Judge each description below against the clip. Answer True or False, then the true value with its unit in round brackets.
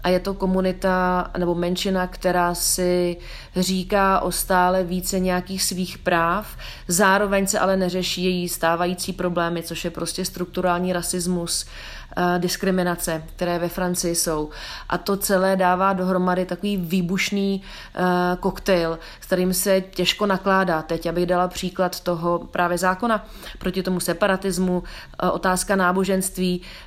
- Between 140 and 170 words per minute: False (125 wpm)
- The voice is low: False (180 Hz)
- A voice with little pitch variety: True (1.2 semitones)